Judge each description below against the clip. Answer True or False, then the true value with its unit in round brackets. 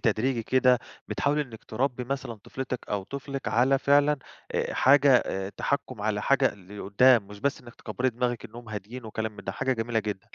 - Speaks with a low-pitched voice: True (120 Hz)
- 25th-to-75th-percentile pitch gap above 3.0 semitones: True (3.6 semitones)